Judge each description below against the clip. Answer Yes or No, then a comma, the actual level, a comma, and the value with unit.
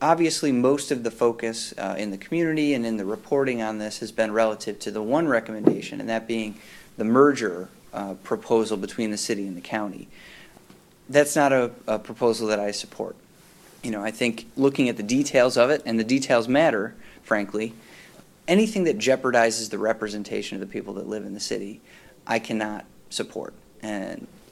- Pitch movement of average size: Yes, average, 4.0 semitones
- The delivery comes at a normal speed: Yes, average, 185 wpm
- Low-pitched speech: Yes, low, 115 Hz